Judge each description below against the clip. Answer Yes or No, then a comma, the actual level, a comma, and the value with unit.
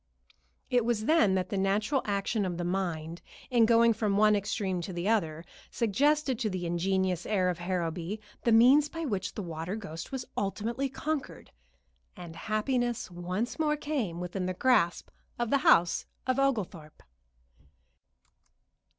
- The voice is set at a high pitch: Yes, high, 205 Hz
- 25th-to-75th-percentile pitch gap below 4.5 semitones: No, average, 5.2 semitones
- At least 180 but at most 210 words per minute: No, average, 150 wpm